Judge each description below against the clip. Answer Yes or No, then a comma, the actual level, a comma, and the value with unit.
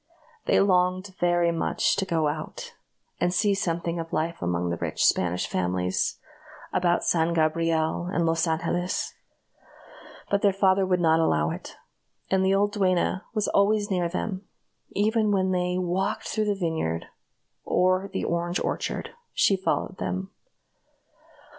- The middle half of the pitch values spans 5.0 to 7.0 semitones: No, average, 2.8 semitones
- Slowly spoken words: No, average, 145 wpm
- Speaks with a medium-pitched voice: Yes, medium, 180 Hz